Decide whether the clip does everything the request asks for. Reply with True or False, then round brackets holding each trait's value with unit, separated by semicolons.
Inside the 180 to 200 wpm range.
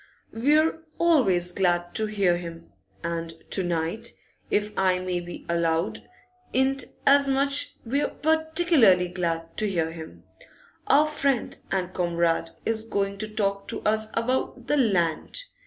False (140 wpm)